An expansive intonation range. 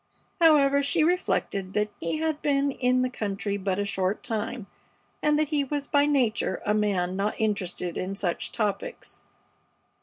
Yes: wide, 6.2 semitones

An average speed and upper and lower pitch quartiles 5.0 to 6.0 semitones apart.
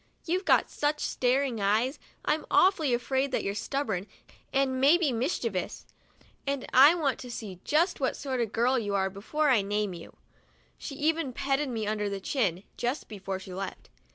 Yes: average, 175 wpm; wide, 5.5 semitones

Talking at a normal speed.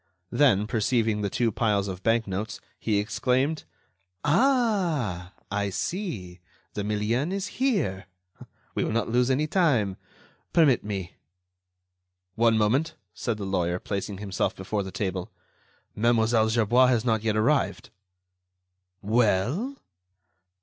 No: slow, 120 wpm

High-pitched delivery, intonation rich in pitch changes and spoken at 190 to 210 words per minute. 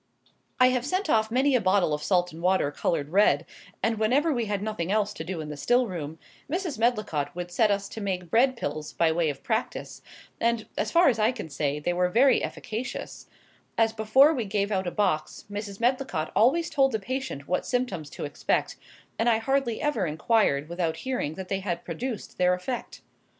Yes: high, 210 Hz; wide, 5.9 semitones; fast, 205 wpm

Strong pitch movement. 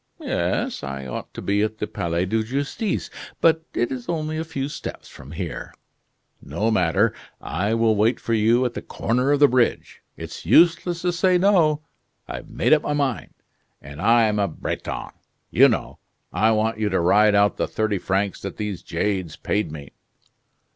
Yes: wide, 6.4 semitones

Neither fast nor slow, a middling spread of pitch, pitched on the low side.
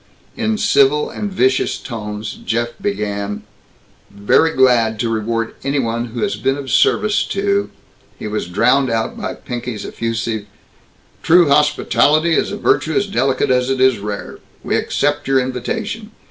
Yes: average, 155 wpm; average, 4.9 semitones; low, 130 Hz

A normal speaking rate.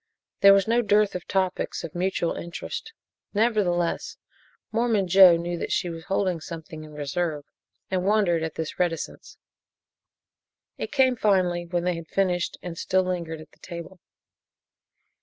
Yes: average, 150 wpm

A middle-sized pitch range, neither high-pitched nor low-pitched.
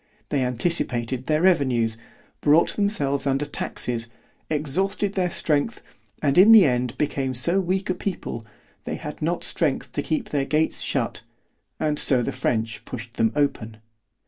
No: wide, 6.2 semitones; medium, 145 Hz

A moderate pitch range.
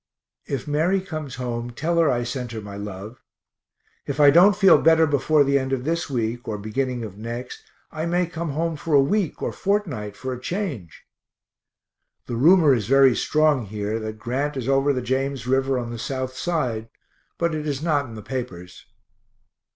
Yes: average, 4.8 semitones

